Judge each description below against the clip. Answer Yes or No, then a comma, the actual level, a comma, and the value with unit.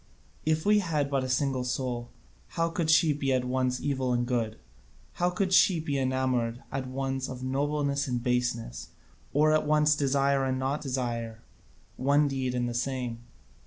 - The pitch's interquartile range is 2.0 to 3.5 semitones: Yes, average, 2.7 semitones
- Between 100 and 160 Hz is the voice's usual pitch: Yes, low, 135 Hz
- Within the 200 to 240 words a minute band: No, average, 170 wpm